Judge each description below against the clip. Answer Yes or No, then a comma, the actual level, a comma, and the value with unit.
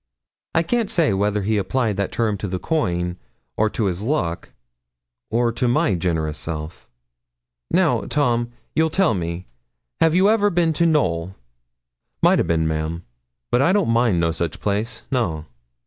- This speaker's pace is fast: No, average, 165 wpm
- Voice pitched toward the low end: Yes, low, 105 Hz